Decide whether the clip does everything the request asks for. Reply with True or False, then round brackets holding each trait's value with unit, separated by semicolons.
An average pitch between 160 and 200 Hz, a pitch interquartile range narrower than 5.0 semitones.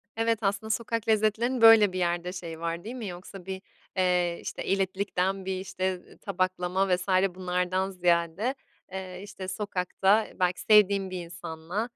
True (190 Hz; 2.4 semitones)